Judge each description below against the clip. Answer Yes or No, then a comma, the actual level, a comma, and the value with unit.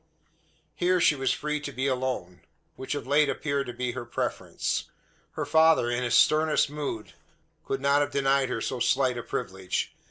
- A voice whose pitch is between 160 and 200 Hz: No, low, 135 Hz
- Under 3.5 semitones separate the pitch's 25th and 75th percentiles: Yes, average, 2.8 semitones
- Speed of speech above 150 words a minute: Yes, average, 180 wpm